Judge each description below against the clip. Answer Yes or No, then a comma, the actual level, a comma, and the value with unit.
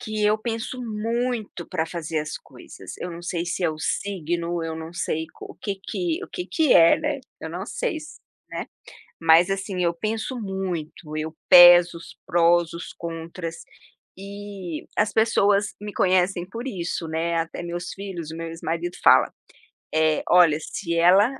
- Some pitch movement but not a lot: Yes, average, 3.6 semitones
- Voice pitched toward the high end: No, medium, 175 Hz